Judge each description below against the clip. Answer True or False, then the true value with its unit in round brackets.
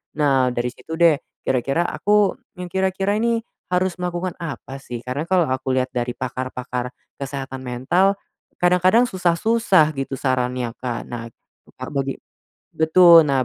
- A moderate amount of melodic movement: False (6.0 semitones)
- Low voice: False (145 Hz)